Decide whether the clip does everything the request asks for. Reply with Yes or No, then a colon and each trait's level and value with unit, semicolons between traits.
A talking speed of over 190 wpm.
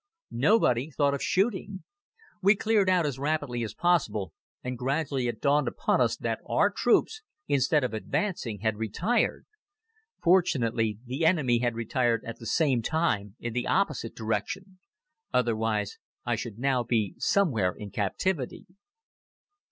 No: average, 140 wpm